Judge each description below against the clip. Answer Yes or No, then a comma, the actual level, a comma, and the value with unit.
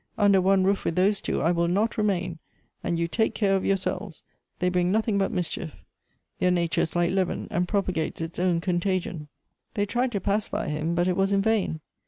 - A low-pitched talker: No, medium, 185 Hz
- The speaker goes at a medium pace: No, fast, 210 wpm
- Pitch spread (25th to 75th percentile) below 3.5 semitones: Yes, narrow, 2.6 semitones